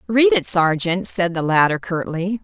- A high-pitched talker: No, medium, 175 Hz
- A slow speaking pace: No, average, 175 wpm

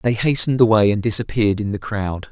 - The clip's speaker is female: No, male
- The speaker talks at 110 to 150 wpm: No, fast, 205 wpm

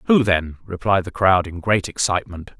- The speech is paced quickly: No, average, 185 wpm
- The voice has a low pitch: Yes, very low, 95 Hz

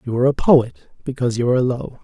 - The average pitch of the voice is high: No, low, 130 Hz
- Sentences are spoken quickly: Yes, fast, 235 wpm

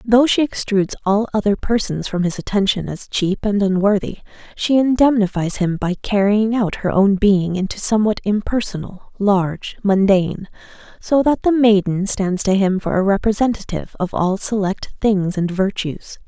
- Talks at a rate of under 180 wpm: Yes, average, 160 wpm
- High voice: Yes, high, 200 Hz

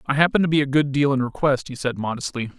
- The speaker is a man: Yes, male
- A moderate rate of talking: No, fast, 280 wpm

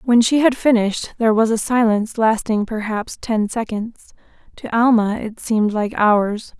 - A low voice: No, high, 225 Hz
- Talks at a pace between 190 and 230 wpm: No, average, 165 wpm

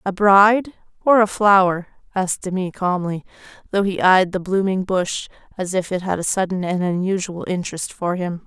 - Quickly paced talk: No, average, 175 wpm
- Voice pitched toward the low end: No, medium, 185 Hz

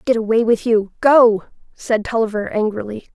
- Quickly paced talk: No, slow, 135 wpm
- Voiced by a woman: Yes, female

